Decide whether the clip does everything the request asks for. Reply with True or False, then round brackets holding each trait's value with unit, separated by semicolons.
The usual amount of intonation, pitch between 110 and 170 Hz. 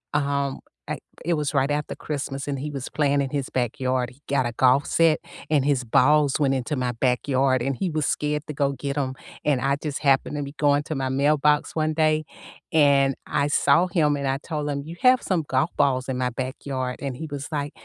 False (2.1 semitones; 140 Hz)